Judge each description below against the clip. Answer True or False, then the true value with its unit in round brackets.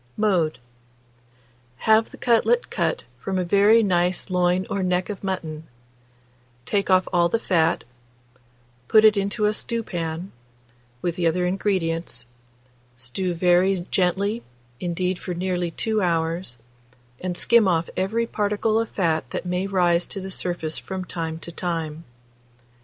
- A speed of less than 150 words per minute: True (140 wpm)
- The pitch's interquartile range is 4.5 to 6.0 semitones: False (2.9 semitones)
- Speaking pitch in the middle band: True (180 Hz)